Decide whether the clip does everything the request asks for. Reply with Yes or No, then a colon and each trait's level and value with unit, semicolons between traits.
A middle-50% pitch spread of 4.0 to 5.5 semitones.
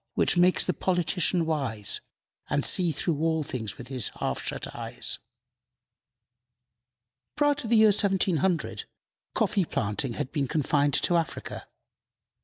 Yes: average, 5.2 semitones